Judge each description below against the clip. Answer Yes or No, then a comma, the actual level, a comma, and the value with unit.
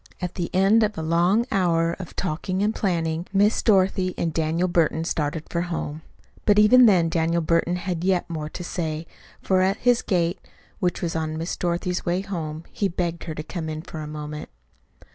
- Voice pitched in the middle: Yes, medium, 175 Hz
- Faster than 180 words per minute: Yes, average, 195 wpm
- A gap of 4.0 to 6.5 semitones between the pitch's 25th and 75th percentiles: No, average, 2.7 semitones